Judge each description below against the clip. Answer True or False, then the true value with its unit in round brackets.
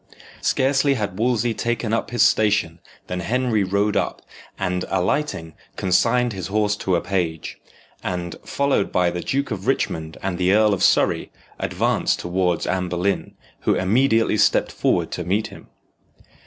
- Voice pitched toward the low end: True (100 Hz)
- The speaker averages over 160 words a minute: False (155 wpm)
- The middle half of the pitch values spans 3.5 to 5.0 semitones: True (4.3 semitones)